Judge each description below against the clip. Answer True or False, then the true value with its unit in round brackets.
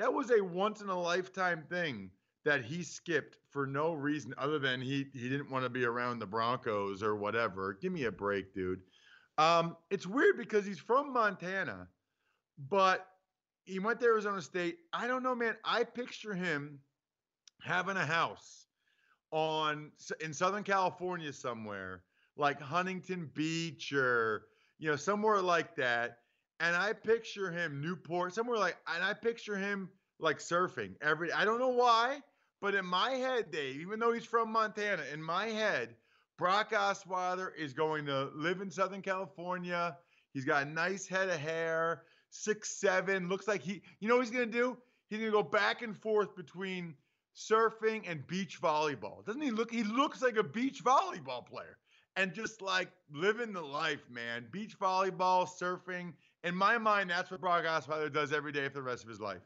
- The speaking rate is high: False (175 wpm)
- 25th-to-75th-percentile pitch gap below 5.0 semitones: False (5.5 semitones)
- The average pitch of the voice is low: False (180 Hz)